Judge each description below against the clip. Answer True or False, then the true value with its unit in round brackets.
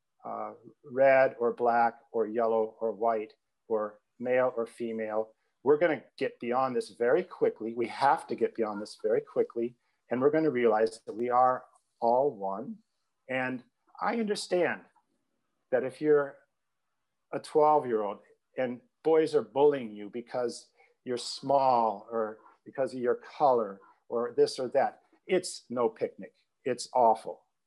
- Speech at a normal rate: True (150 wpm)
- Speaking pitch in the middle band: False (125 Hz)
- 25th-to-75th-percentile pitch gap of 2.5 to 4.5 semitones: False (5.4 semitones)